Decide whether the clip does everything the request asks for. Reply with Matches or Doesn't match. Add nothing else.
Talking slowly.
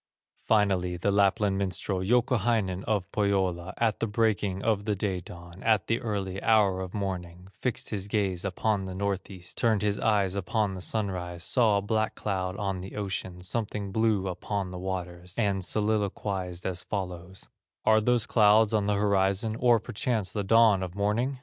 Doesn't match